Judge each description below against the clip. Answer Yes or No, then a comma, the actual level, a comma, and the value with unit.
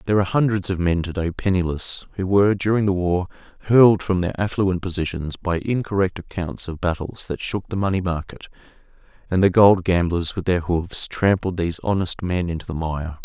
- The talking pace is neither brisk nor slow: Yes, average, 190 wpm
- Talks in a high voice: No, very low, 90 Hz